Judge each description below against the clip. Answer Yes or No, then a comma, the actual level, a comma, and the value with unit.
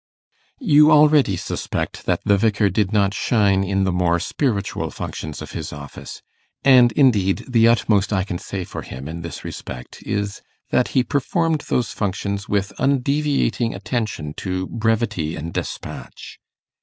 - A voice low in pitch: Yes, low, 100 Hz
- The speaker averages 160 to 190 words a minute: No, average, 150 wpm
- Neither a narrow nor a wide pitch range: Yes, average, 5.0 semitones